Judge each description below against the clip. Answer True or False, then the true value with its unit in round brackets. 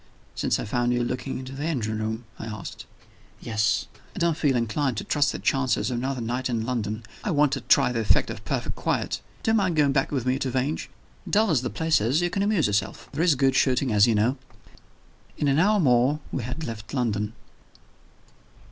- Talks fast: True (215 wpm)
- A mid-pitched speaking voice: False (130 Hz)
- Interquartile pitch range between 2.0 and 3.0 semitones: False (4.2 semitones)